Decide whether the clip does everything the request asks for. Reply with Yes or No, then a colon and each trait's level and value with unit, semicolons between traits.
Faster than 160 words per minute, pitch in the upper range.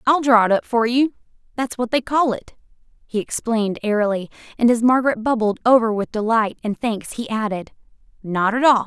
Yes: average, 185 wpm; high, 230 Hz